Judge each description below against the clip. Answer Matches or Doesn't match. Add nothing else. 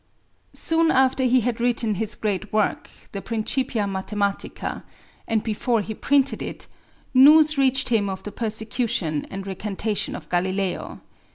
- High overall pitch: Matches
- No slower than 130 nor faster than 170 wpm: Matches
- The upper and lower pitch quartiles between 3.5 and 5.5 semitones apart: Matches